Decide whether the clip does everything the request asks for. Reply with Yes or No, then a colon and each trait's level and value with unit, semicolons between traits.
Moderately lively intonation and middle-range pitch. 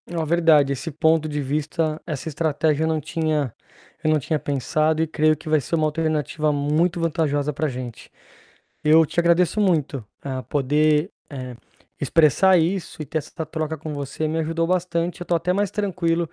No: narrow, 2.1 semitones; medium, 155 Hz